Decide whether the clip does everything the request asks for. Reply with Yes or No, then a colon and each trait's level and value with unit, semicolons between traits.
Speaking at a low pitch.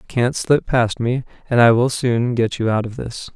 Yes: low, 120 Hz